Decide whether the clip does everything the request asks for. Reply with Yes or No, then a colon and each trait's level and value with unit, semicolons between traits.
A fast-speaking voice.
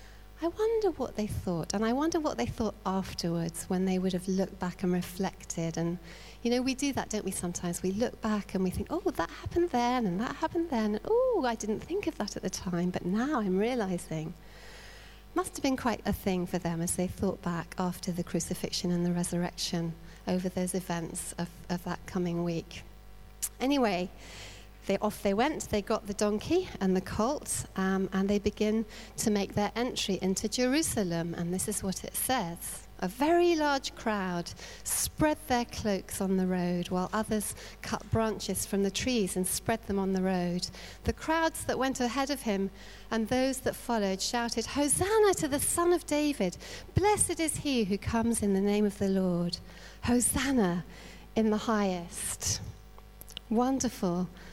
No: average, 185 wpm